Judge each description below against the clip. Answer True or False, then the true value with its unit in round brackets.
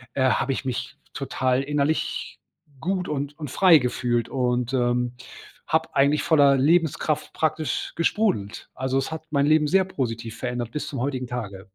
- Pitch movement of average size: True (4.0 semitones)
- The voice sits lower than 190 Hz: True (140 Hz)